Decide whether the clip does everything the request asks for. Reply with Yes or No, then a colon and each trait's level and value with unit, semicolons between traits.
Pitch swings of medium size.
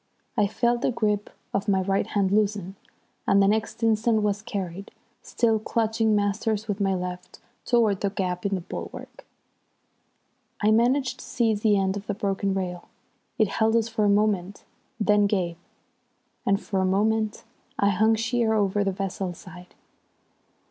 No: narrow, 2.2 semitones